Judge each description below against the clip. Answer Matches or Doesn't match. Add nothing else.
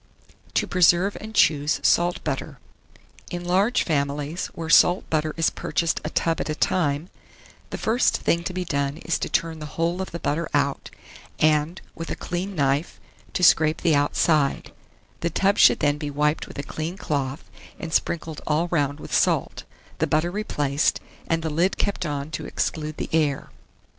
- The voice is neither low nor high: Matches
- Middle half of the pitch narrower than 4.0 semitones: Matches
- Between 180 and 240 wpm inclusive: Matches